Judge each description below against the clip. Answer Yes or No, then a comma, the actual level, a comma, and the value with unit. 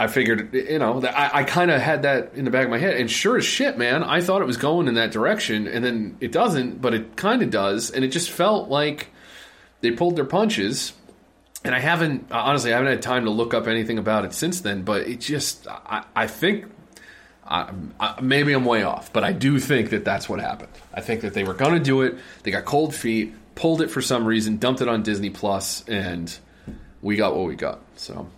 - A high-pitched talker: No, low, 125 Hz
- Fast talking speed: Yes, fast, 245 wpm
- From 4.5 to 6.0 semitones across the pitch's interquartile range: Yes, average, 5.0 semitones